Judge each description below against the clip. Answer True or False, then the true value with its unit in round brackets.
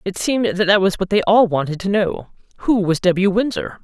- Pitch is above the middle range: True (195 Hz)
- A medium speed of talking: False (235 wpm)